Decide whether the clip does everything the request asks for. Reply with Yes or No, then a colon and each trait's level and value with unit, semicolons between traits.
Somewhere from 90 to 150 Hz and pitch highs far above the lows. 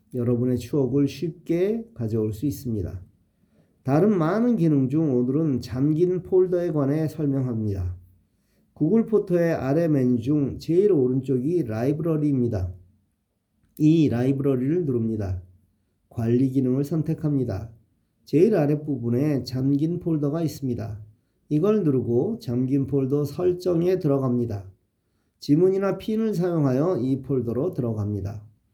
Yes: low, 135 Hz; wide, 5.7 semitones